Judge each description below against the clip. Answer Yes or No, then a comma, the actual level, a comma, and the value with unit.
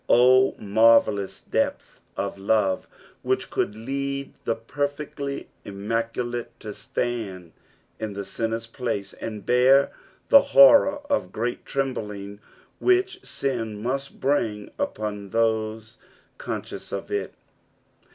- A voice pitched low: Yes, low, 115 Hz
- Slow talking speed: Yes, slow, 110 wpm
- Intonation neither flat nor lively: Yes, average, 4.6 semitones